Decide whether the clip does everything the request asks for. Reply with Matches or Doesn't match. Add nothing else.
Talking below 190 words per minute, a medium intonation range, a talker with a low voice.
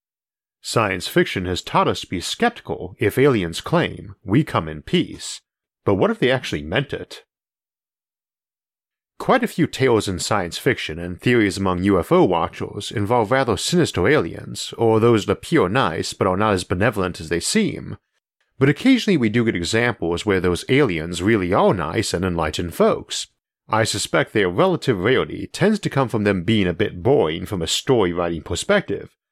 Doesn't match